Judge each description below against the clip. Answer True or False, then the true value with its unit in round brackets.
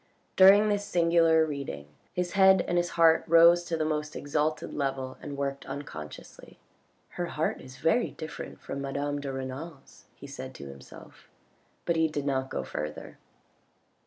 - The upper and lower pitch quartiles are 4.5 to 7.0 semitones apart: False (3.6 semitones)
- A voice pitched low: False (150 Hz)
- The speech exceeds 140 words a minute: True (165 wpm)